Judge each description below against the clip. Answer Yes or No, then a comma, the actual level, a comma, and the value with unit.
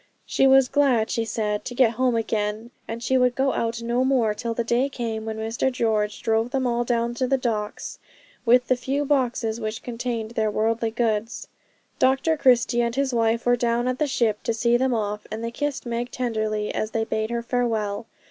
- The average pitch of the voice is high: Yes, high, 235 Hz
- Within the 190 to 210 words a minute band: Yes, fast, 205 wpm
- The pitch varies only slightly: Yes, narrow, 2.2 semitones